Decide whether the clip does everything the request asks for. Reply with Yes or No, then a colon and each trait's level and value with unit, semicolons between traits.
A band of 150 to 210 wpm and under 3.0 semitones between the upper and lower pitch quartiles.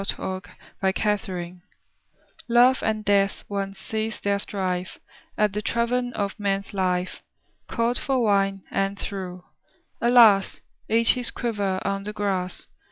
No: slow, 135 wpm; narrow, 2.5 semitones